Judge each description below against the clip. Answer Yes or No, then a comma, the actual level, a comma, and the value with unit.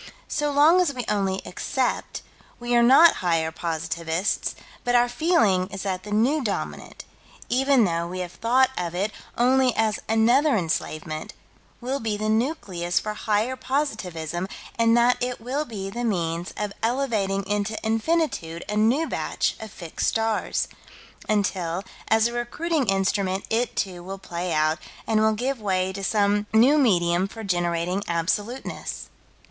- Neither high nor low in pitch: No, high, 210 Hz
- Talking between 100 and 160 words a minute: Yes, average, 150 wpm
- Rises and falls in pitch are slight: No, average, 4.8 semitones